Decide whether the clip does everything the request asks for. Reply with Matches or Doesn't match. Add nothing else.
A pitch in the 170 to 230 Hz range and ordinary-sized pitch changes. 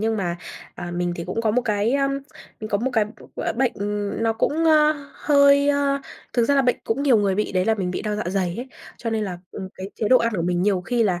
Matches